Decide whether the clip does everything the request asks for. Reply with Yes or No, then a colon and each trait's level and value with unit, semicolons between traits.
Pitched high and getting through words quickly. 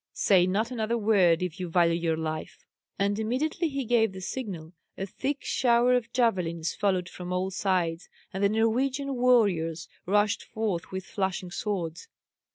No: high, 195 Hz; average, 160 wpm